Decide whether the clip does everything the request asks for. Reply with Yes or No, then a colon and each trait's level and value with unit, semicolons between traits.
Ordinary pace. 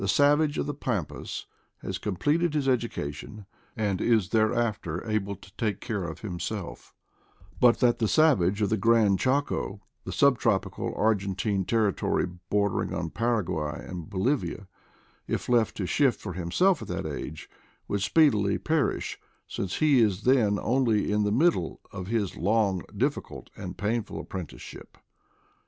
Yes: average, 150 wpm